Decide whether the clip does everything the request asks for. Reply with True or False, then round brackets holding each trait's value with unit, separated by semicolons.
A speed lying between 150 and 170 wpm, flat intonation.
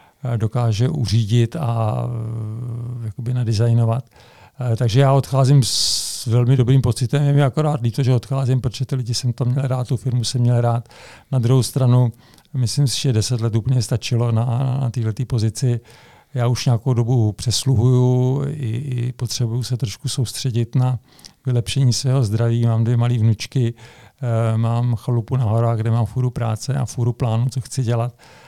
True (160 wpm; 1.8 semitones)